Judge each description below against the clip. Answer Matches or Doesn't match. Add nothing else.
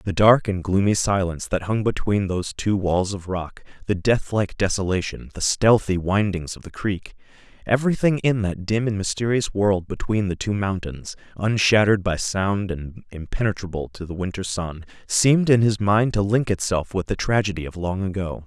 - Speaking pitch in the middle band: Doesn't match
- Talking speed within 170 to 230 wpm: Matches